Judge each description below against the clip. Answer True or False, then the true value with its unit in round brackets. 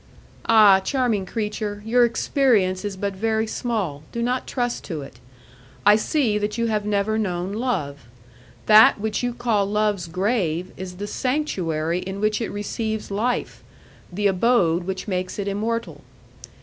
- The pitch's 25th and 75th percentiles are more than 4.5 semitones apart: False (3.5 semitones)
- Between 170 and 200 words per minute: False (150 wpm)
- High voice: True (210 Hz)